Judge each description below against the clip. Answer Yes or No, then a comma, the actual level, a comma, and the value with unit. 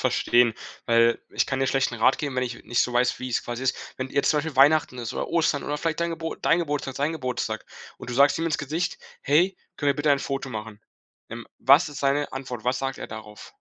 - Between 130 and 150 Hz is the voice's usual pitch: Yes, low, 135 Hz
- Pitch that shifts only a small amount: No, average, 3.2 semitones